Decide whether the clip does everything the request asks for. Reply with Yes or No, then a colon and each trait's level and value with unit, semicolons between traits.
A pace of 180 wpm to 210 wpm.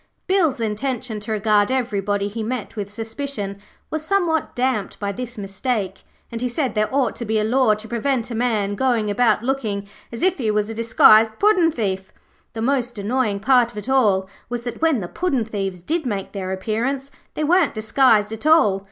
Yes: average, 195 wpm